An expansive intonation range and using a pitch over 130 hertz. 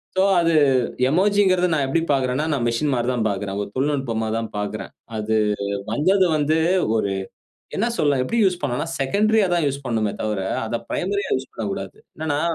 Yes: wide, 7.1 semitones; medium, 140 Hz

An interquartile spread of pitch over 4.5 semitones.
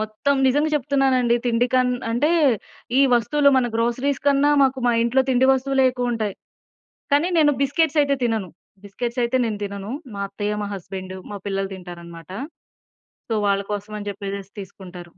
Yes: average, 5.0 semitones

